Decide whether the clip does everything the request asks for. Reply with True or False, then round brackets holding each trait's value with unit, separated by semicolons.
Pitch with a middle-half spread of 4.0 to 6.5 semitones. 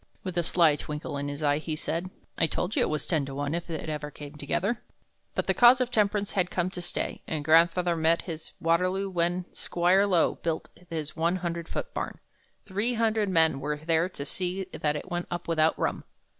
False (3.0 semitones)